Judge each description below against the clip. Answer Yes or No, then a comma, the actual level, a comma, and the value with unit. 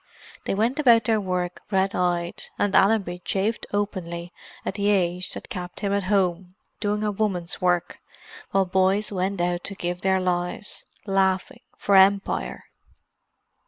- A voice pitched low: No, high, 190 Hz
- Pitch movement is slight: Yes, narrow, 2.3 semitones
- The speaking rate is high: No, average, 150 wpm